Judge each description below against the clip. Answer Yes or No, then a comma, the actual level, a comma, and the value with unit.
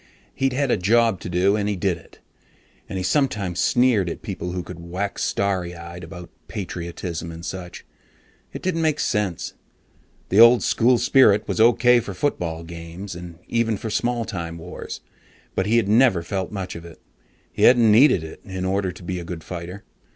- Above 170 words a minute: Yes, average, 190 wpm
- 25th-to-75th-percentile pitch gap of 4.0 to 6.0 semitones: Yes, average, 4.7 semitones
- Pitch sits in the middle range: No, very low, 95 Hz